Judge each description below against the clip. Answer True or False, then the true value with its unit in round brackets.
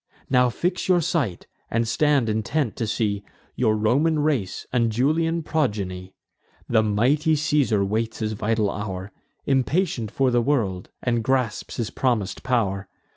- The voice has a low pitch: True (115 Hz)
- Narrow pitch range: False (5.3 semitones)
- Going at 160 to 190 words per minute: False (140 wpm)